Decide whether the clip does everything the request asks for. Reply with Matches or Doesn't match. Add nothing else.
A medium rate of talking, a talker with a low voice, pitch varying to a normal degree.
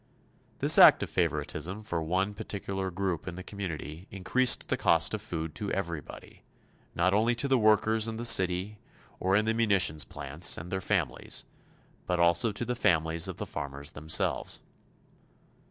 Matches